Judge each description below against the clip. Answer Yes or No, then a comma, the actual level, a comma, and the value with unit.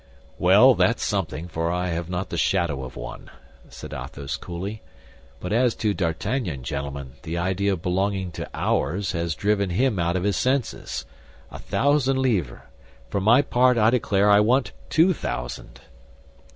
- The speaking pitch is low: Yes, very low, 95 Hz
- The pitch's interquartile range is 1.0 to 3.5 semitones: No, average, 4.7 semitones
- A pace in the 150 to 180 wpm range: Yes, average, 160 wpm